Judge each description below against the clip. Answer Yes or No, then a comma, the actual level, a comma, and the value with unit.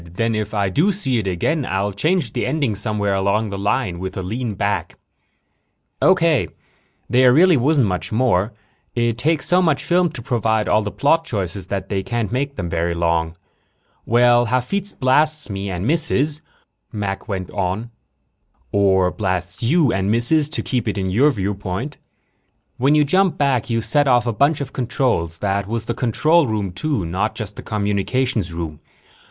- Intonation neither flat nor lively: No, wide, 6.1 semitones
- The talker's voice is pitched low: Yes, low, 115 Hz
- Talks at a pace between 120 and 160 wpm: No, average, 175 wpm